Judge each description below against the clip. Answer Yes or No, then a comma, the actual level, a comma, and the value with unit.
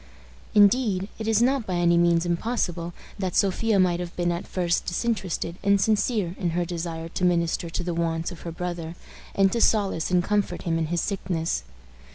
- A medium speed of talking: Yes, average, 190 wpm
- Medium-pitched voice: Yes, medium, 175 Hz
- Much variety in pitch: No, average, 2.8 semitones